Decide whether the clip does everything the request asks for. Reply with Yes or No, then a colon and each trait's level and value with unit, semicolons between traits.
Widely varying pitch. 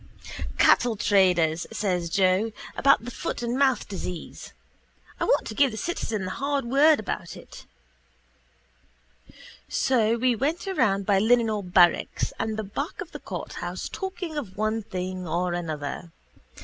Yes: wide, 6.2 semitones